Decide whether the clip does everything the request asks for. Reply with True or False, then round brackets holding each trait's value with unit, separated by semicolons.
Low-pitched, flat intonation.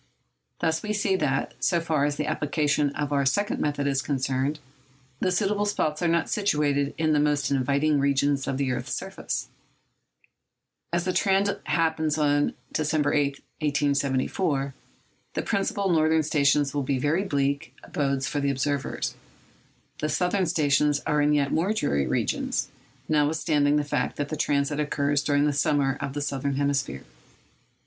False (145 Hz; 2.0 semitones)